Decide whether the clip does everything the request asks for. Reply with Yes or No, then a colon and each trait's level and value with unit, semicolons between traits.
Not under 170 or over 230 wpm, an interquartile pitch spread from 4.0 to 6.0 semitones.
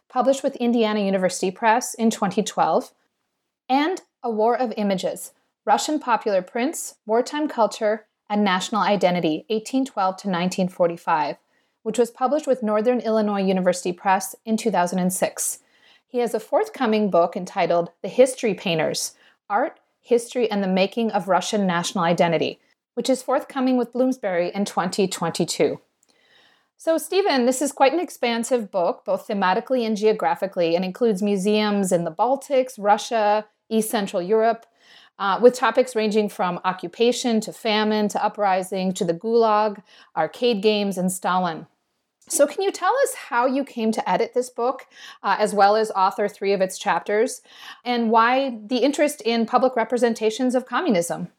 No: average, 150 wpm; average, 4.3 semitones